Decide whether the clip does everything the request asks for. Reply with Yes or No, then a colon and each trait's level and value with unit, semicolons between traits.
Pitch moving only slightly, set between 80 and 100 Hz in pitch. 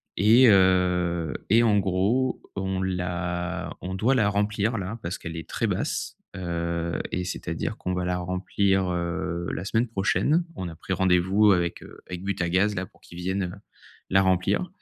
Yes: narrow, 2.3 semitones; very low, 95 Hz